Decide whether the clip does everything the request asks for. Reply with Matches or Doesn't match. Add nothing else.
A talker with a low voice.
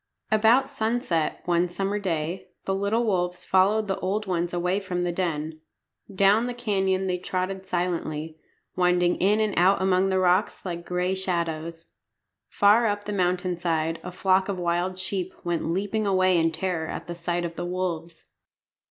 Doesn't match